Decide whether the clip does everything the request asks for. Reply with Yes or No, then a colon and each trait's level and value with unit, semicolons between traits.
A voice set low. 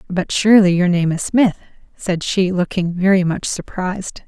No: medium, 185 Hz